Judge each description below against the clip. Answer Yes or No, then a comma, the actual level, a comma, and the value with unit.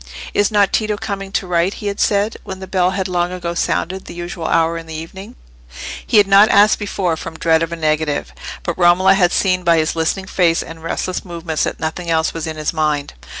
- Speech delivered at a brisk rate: Yes, fast, 225 wpm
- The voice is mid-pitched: Yes, medium, 175 Hz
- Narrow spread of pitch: No, average, 3.0 semitones